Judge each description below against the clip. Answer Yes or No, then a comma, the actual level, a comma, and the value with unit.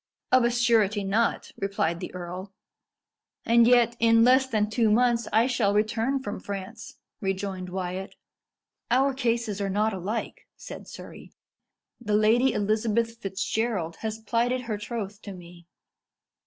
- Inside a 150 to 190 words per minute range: No, average, 140 wpm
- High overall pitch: Yes, high, 215 Hz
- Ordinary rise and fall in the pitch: Yes, average, 3.1 semitones